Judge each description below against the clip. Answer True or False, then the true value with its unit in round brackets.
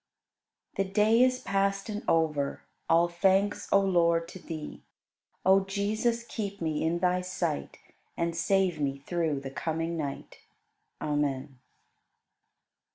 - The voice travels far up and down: False (3.7 semitones)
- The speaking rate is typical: False (130 wpm)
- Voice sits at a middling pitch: True (175 Hz)